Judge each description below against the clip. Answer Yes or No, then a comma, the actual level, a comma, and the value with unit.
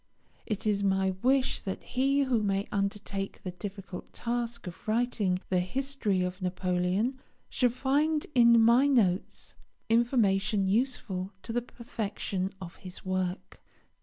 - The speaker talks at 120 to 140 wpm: Yes, slow, 135 wpm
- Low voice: No, high, 210 Hz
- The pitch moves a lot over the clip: No, average, 4.3 semitones